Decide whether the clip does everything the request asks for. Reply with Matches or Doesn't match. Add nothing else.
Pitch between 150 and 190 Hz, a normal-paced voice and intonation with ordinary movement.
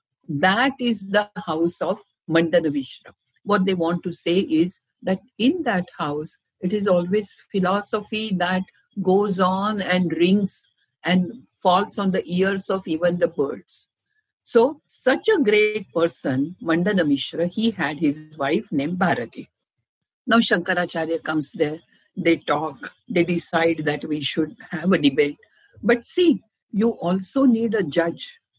Matches